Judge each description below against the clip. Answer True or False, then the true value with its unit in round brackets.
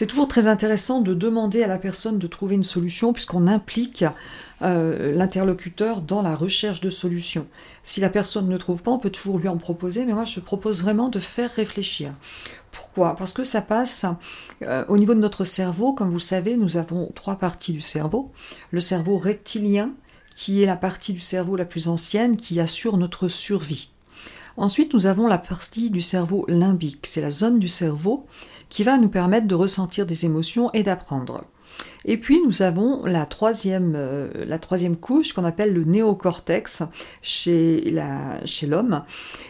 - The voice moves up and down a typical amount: True (3.7 semitones)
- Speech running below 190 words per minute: True (180 wpm)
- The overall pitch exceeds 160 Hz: True (190 Hz)